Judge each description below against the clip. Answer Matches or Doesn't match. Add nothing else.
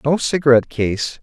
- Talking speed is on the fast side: Doesn't match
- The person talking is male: Matches